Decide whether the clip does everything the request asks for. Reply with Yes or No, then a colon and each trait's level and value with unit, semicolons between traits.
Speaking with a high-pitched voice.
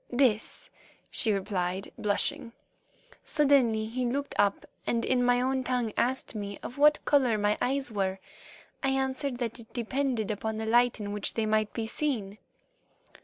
Yes: high, 235 Hz